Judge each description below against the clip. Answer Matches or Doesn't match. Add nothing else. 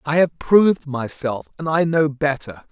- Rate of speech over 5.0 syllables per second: Doesn't match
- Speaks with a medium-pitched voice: Matches